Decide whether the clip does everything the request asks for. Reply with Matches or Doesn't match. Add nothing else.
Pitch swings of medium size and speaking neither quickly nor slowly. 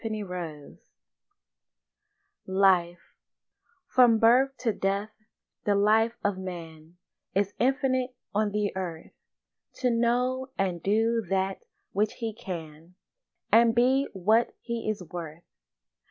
Doesn't match